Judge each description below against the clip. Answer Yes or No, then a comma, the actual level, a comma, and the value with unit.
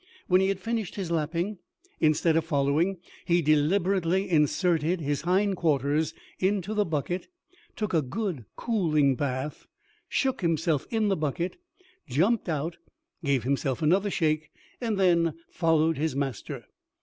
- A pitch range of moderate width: Yes, average, 4.1 semitones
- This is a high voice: No, medium, 165 Hz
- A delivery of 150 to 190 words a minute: No, slow, 135 wpm